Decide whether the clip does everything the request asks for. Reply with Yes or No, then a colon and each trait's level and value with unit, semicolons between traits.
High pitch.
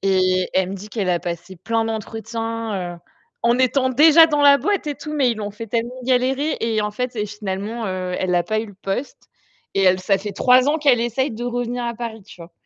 Yes: high, 225 Hz